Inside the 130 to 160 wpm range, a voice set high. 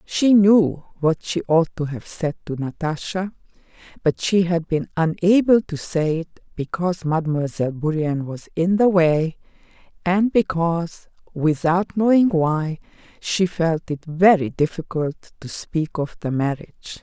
No: average, 140 wpm; medium, 170 Hz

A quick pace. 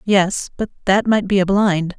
Yes: fast, 210 wpm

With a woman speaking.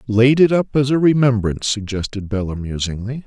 No: male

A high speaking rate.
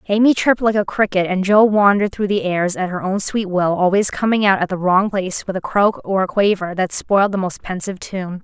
Yes: fast, 250 wpm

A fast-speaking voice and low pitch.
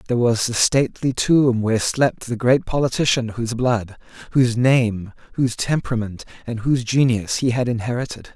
No: average, 160 wpm; low, 120 Hz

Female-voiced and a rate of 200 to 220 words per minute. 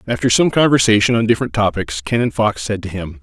No: male; fast, 205 wpm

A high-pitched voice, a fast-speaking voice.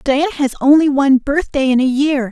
Yes: very high, 275 Hz; fast, 210 wpm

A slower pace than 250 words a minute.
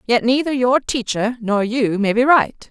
Yes: average, 200 wpm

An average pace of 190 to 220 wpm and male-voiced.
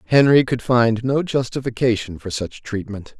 No: average, 150 wpm; male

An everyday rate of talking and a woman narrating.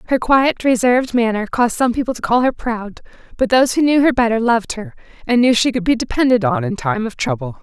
No: fast, 235 wpm; female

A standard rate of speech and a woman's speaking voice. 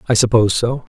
No: average, 190 wpm; male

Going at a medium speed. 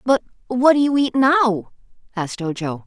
Yes: average, 165 wpm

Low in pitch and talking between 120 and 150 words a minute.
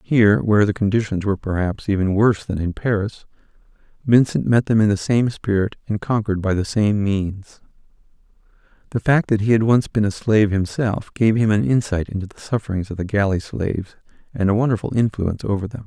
No: low, 105 Hz; average, 195 wpm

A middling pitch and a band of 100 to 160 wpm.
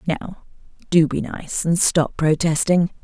Yes: medium, 165 Hz; average, 140 wpm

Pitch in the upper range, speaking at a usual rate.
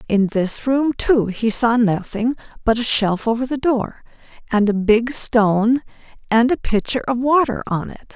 Yes: high, 230 Hz; average, 175 wpm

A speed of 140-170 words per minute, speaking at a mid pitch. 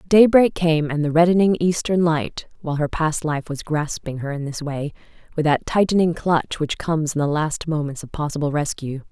No: fast, 205 wpm; medium, 155 Hz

